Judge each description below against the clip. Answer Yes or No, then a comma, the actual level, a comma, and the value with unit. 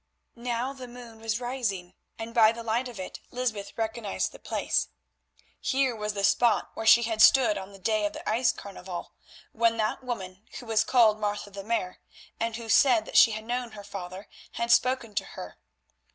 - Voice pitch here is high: Yes, high, 225 Hz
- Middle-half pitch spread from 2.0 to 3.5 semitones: Yes, narrow, 2.6 semitones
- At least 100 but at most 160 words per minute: No, average, 195 wpm